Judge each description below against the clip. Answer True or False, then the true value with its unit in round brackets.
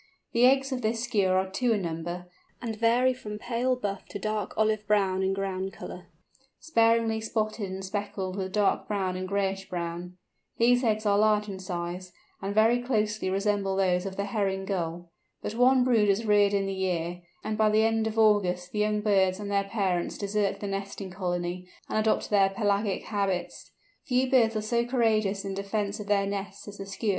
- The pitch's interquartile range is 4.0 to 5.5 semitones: False (2.4 semitones)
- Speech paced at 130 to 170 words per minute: False (195 wpm)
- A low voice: False (205 Hz)